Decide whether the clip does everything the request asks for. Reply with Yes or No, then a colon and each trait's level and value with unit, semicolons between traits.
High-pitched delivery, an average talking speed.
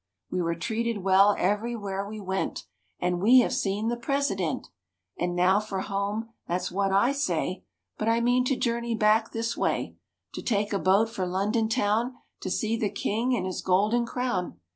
Yes: high, 210 Hz; average, 180 wpm